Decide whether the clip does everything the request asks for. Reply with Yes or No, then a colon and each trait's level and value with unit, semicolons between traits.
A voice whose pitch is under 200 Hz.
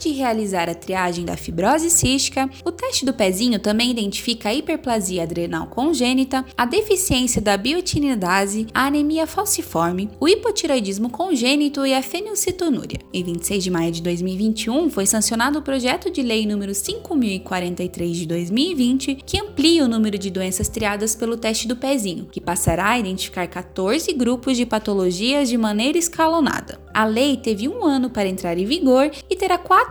No: high, 245 Hz